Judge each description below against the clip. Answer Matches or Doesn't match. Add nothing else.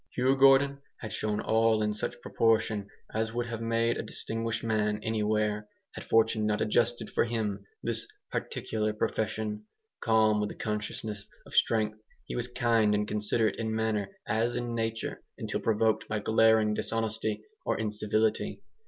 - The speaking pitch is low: Matches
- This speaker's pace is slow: Doesn't match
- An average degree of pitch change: Doesn't match